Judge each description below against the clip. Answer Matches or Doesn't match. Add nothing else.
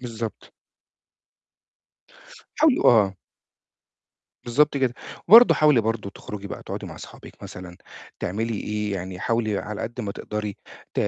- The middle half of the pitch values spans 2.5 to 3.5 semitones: Matches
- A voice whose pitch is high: Doesn't match